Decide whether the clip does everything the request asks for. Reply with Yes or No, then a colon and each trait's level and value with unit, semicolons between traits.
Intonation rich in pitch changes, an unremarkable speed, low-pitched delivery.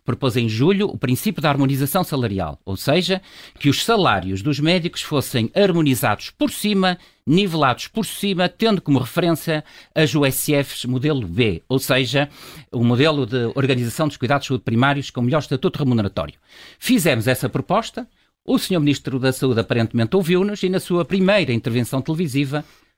No: wide, 5.9 semitones; average, 155 wpm; medium, 145 Hz